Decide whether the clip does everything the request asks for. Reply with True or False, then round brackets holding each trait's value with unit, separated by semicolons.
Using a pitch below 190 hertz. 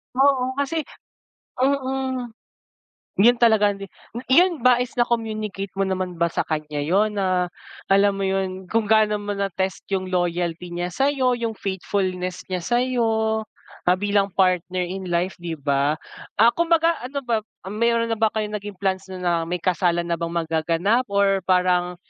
False (195 Hz)